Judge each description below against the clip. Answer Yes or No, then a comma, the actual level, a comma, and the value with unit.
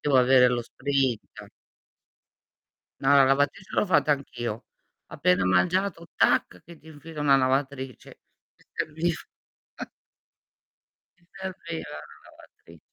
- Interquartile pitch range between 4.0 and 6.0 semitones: Yes, average, 4.4 semitones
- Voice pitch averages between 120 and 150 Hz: Yes, medium, 140 Hz